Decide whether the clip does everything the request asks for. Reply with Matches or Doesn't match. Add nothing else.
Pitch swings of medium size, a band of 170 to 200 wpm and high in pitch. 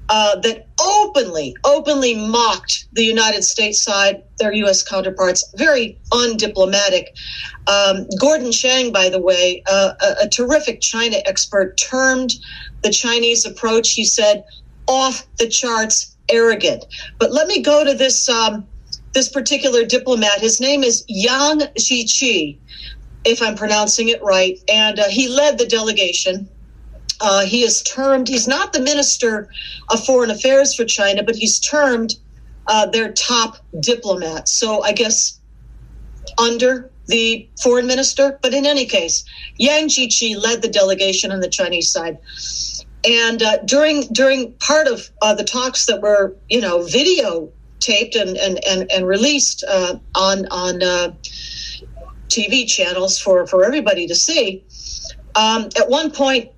Doesn't match